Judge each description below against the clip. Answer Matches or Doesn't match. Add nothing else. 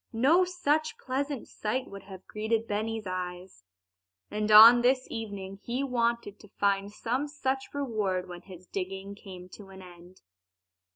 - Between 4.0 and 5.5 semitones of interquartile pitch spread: Matches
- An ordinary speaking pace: Matches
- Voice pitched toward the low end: Doesn't match